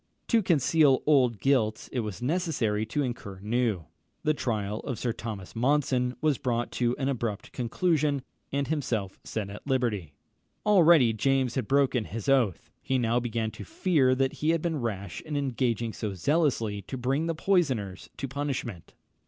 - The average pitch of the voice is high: No, low, 125 Hz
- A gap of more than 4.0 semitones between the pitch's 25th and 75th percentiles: Yes, average, 4.4 semitones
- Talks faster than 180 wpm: No, average, 165 wpm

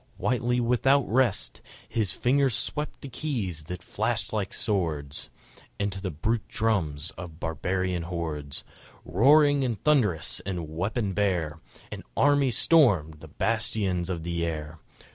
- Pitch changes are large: Yes, wide, 6.9 semitones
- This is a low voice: Yes, very low, 95 Hz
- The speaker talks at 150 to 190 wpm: No, slow, 135 wpm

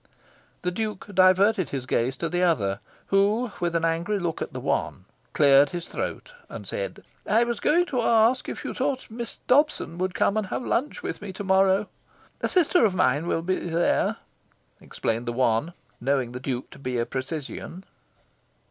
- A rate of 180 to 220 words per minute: Yes, average, 185 wpm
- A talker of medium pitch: Yes, medium, 180 Hz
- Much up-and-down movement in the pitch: Yes, wide, 7.5 semitones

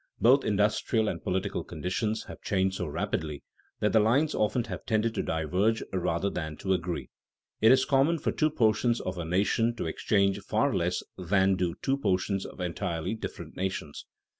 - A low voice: Yes, low, 100 Hz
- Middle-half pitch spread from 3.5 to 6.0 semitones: Yes, average, 3.8 semitones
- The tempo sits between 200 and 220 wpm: No, average, 175 wpm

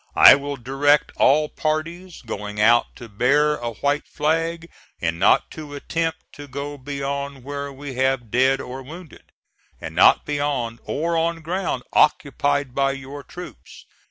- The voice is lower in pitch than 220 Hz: Yes, medium, 140 Hz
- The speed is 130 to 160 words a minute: Yes, average, 150 wpm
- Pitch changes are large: No, narrow, 2.5 semitones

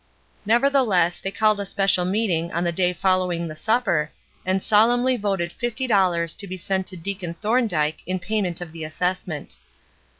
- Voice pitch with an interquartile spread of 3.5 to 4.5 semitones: Yes, average, 3.8 semitones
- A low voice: No, medium, 185 Hz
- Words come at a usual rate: Yes, average, 170 wpm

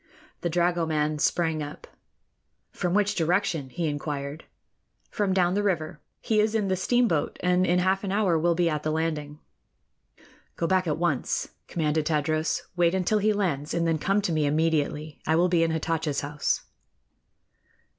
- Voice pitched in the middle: Yes, medium, 165 Hz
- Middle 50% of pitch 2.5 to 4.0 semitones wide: Yes, average, 3.2 semitones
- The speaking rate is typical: Yes, average, 165 wpm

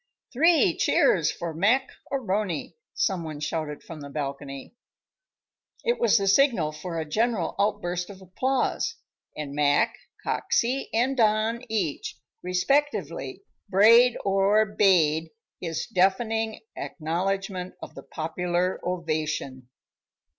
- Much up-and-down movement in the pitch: Yes, wide, 5.7 semitones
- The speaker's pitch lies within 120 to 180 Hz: No, high, 190 Hz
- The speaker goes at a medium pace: No, slow, 110 wpm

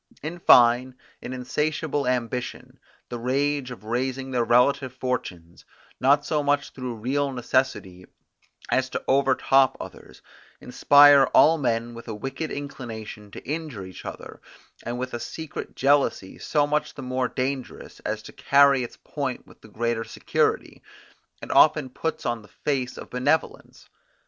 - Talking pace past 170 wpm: No, average, 150 wpm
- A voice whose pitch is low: Yes, low, 130 Hz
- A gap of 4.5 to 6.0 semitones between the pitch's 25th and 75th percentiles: No, average, 3.1 semitones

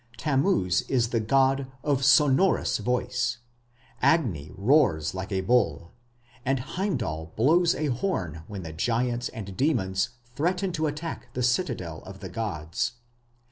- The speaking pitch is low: Yes, low, 125 Hz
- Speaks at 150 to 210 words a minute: No, slow, 135 wpm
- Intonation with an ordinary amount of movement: No, wide, 7.0 semitones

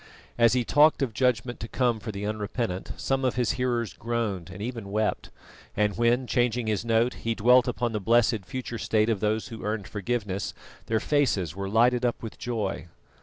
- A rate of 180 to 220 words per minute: Yes, average, 190 wpm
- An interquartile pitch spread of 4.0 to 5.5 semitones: No, narrow, 2.6 semitones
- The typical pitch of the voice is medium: No, low, 115 Hz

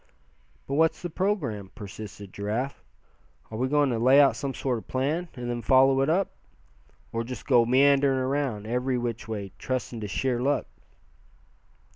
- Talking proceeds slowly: No, average, 165 wpm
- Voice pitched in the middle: No, low, 130 Hz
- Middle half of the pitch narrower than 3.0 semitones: No, average, 3.3 semitones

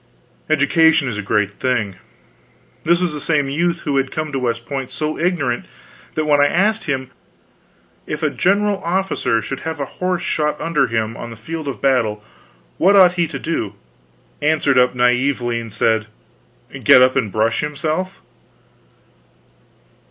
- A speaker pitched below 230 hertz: Yes, medium, 140 Hz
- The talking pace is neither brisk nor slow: Yes, average, 160 wpm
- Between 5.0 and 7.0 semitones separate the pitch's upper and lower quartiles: Yes, average, 5.3 semitones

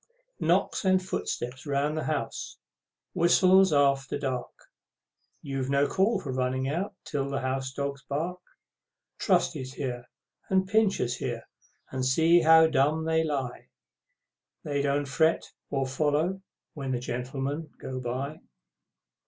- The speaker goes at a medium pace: No, slow, 130 wpm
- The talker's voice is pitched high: No, medium, 140 Hz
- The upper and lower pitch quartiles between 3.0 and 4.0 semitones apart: Yes, average, 3.6 semitones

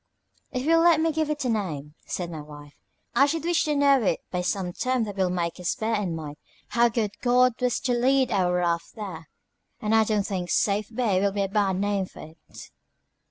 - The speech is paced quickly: Yes, fast, 225 wpm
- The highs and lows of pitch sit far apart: Yes, wide, 5.9 semitones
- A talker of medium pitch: No, high, 205 Hz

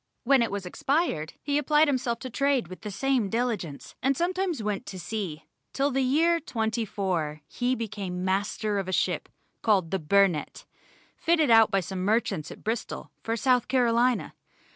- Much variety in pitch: Yes, wide, 5.7 semitones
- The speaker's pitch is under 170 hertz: No, high, 225 Hz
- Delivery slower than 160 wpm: No, average, 170 wpm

